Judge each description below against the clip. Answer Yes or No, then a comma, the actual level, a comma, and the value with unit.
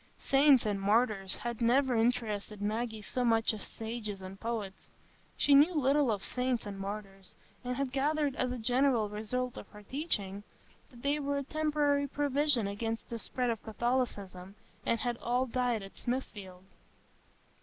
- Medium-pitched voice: No, high, 235 Hz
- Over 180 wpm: No, average, 160 wpm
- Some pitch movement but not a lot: Yes, average, 4.1 semitones